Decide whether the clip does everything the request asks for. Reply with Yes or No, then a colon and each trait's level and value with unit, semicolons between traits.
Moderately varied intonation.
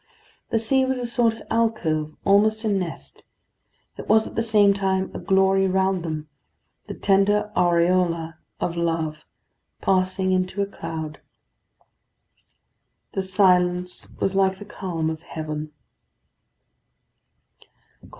Yes: average, 3.2 semitones